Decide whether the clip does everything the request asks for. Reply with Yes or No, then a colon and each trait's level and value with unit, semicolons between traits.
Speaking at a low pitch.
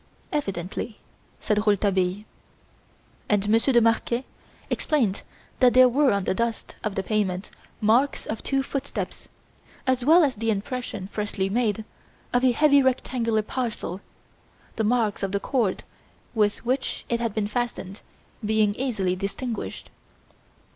No: high, 220 Hz